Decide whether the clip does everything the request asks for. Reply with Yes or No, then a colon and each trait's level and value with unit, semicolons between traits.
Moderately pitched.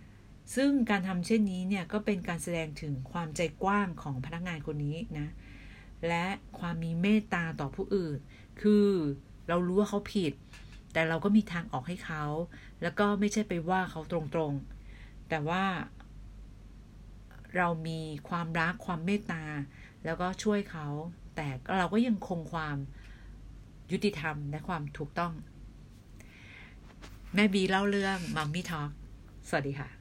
Yes: medium, 165 Hz